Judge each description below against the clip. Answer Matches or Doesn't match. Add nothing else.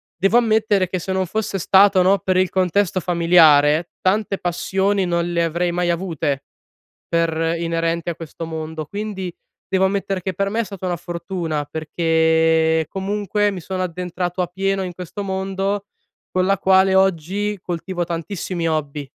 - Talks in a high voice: Doesn't match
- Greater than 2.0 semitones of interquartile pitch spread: Matches